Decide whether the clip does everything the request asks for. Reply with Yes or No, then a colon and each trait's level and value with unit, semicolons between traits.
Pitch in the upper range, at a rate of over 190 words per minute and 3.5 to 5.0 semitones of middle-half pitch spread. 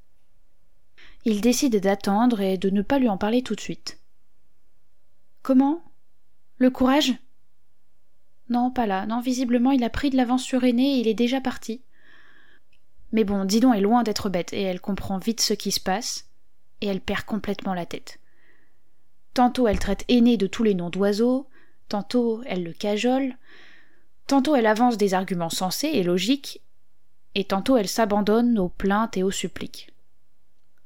No: high, 230 Hz; average, 165 wpm; average, 4.3 semitones